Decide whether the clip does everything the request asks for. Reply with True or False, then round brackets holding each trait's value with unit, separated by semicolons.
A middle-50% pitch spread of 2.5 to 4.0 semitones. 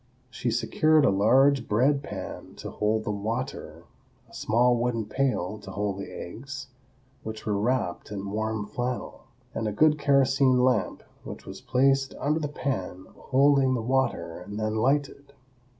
False (4.5 semitones)